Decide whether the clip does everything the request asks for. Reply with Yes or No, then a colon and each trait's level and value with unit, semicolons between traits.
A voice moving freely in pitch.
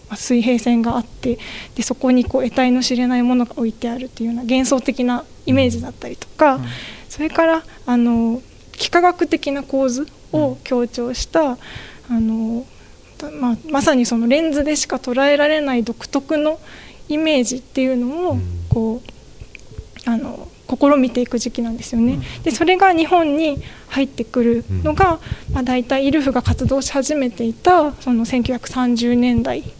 No: average, 3.5 semitones